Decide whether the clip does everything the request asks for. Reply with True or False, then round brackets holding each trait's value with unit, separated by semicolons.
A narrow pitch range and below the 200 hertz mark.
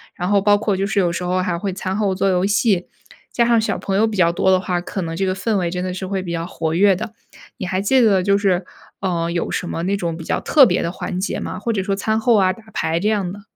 True (2.3 semitones; 190 Hz)